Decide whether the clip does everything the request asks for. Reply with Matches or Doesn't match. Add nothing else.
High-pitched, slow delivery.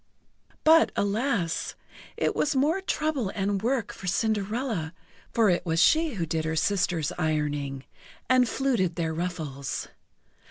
Matches